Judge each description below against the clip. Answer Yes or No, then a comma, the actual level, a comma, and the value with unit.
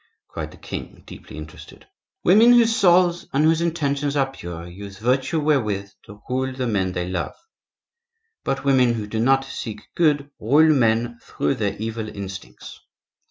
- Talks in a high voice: No, low, 125 Hz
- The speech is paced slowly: No, average, 160 wpm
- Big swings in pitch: Yes, wide, 6.0 semitones